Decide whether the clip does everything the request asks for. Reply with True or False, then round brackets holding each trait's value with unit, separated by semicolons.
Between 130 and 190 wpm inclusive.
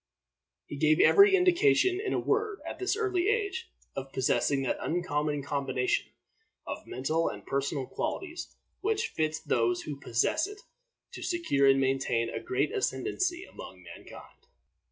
True (145 wpm)